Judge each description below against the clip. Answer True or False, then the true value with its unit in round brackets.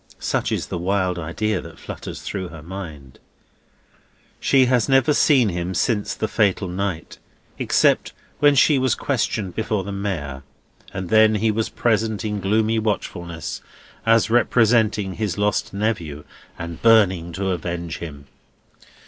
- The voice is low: True (100 Hz)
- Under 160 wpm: True (140 wpm)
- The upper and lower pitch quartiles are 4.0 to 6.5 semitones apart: True (4.3 semitones)